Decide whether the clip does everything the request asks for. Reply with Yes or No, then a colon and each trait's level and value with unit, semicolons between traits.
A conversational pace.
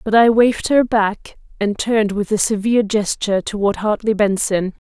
Yes: average, 170 wpm